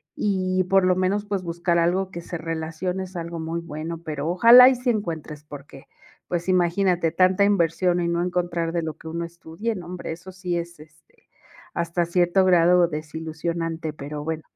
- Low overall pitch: No, medium, 170 Hz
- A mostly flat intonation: Yes, narrow, 2.2 semitones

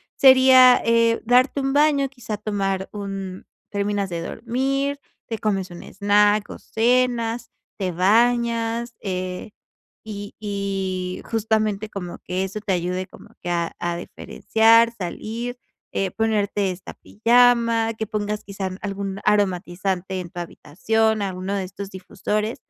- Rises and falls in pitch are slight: No, average, 3.3 semitones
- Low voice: No, high, 210 Hz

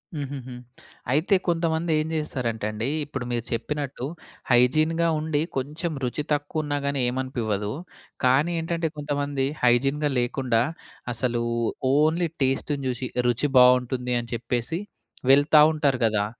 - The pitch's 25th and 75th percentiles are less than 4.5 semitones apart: Yes, average, 3.7 semitones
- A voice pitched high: No, low, 135 Hz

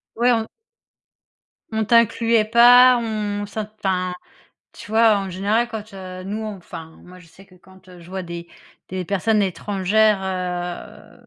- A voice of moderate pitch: No, high, 200 Hz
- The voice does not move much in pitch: No, average, 3.2 semitones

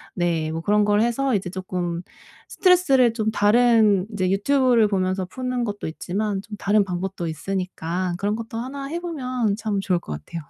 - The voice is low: No, high, 205 Hz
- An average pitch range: Yes, average, 4.4 semitones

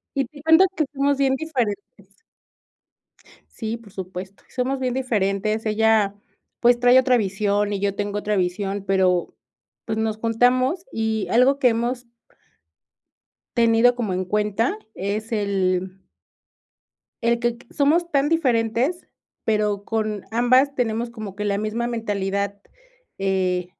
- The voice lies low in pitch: No, high, 220 Hz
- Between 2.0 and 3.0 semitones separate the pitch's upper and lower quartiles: No, average, 3.6 semitones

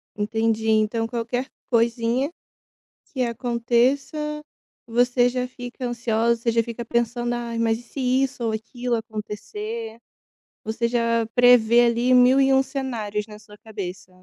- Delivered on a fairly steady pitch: Yes, narrow, 1.8 semitones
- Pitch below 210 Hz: No, high, 235 Hz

